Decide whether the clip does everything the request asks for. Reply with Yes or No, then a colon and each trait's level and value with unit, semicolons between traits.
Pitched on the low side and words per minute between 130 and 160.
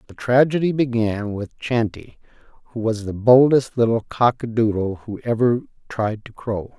Yes: low, 115 Hz; average, 140 wpm